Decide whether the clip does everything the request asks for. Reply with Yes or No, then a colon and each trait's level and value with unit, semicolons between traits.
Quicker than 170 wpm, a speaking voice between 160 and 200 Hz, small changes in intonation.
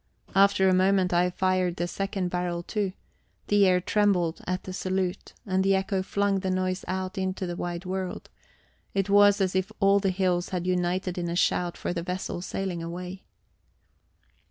Yes: average, 180 wpm; medium, 185 Hz; narrow, 1.4 semitones